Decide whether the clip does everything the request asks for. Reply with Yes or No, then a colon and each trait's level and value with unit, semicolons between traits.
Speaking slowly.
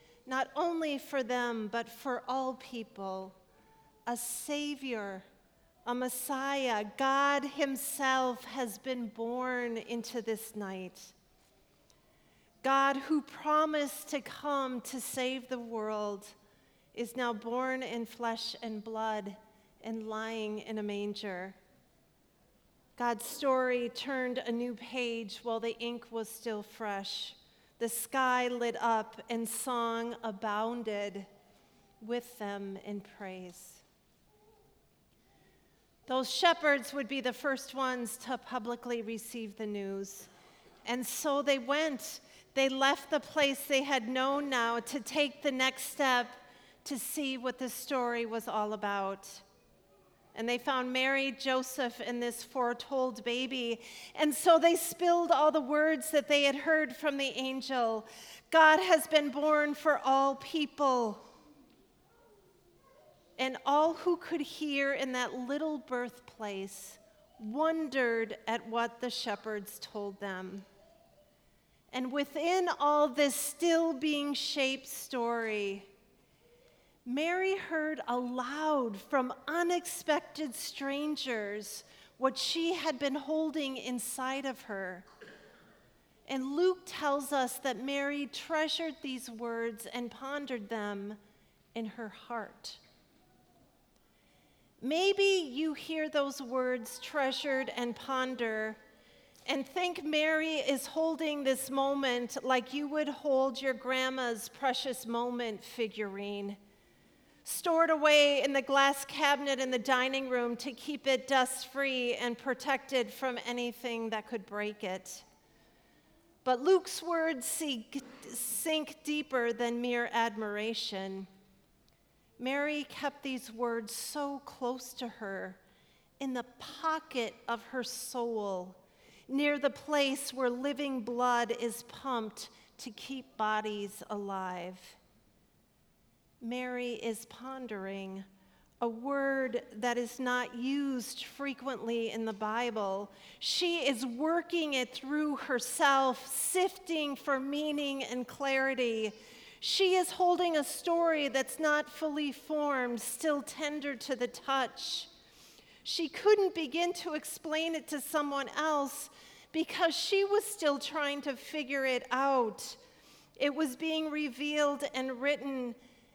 Yes: slow, 120 wpm